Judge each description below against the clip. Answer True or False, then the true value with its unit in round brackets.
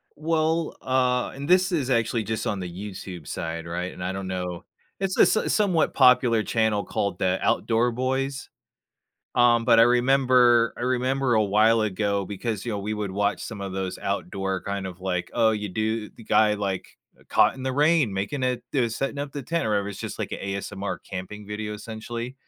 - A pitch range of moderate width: True (4.4 semitones)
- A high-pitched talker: False (110 Hz)